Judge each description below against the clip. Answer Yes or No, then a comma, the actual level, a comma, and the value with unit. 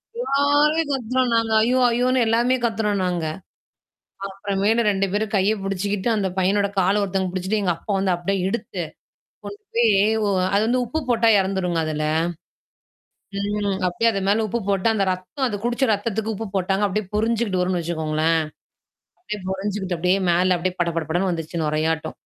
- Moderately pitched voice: No, high, 200 Hz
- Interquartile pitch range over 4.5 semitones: No, average, 3.8 semitones